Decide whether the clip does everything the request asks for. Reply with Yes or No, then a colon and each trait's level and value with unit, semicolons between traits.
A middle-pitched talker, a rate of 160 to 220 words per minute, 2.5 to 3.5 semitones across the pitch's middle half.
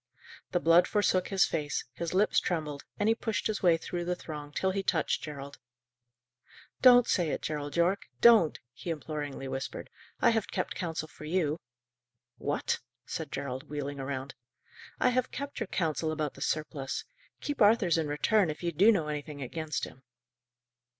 No: medium, 160 Hz; average, 170 wpm; average, 4.5 semitones